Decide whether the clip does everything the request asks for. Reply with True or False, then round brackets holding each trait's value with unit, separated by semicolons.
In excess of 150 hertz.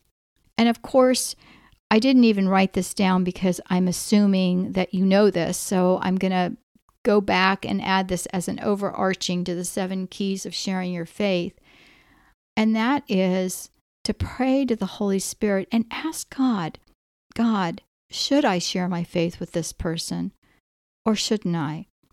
True (190 Hz)